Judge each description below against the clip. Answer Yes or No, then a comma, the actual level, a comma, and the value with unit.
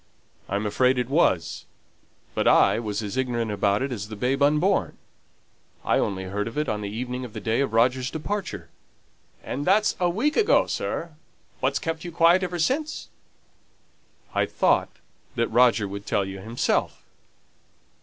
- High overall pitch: No, low, 125 Hz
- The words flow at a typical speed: Yes, average, 165 wpm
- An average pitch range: No, wide, 7.4 semitones